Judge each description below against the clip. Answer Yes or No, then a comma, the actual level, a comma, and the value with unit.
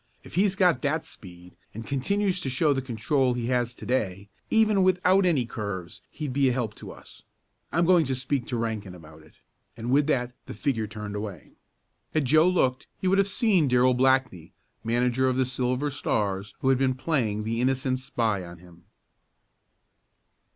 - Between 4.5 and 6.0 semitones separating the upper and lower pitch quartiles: Yes, average, 5.2 semitones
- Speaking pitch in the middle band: No, low, 130 Hz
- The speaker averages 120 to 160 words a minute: No, average, 185 wpm